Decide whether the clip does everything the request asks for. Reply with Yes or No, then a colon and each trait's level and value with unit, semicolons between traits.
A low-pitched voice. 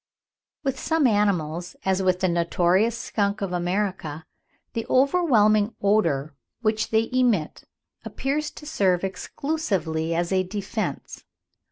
No: high, 200 Hz